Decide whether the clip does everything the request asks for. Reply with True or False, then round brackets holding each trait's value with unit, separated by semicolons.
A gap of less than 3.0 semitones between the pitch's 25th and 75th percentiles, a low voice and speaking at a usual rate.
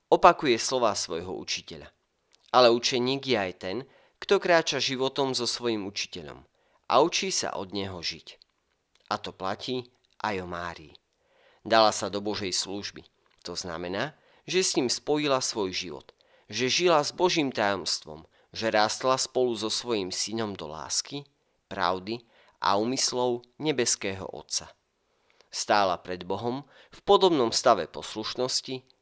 False (5.1 semitones; 115 Hz; 135 wpm)